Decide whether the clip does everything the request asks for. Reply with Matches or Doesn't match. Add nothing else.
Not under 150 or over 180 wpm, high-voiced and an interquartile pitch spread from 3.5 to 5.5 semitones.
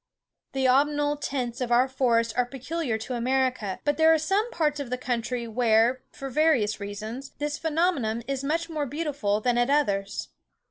Matches